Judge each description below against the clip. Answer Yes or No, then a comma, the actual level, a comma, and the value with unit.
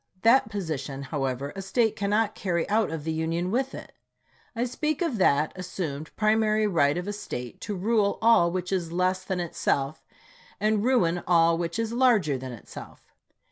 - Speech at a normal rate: Yes, average, 175 wpm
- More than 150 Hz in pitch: Yes, medium, 185 Hz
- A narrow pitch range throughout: No, average, 5.2 semitones